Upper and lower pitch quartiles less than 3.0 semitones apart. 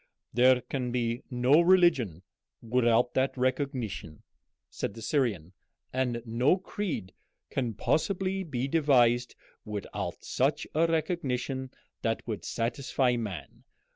No: average, 3.8 semitones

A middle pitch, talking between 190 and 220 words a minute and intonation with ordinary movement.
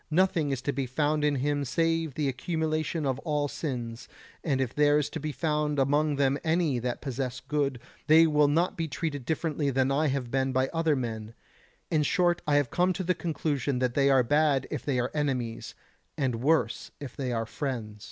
Yes: medium, 145 Hz; average, 200 wpm; average, 3.0 semitones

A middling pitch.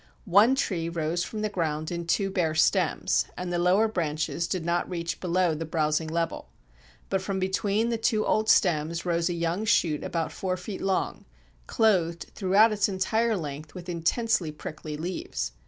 Yes: medium, 175 Hz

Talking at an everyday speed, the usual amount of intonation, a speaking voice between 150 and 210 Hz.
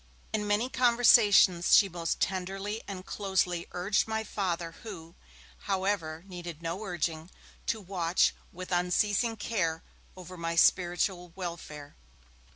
No: slow, 120 wpm; average, 3.3 semitones; medium, 185 Hz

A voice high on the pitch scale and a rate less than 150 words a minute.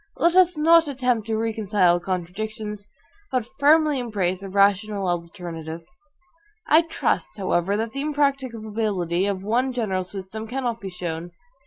Yes: high, 210 Hz; slow, 135 wpm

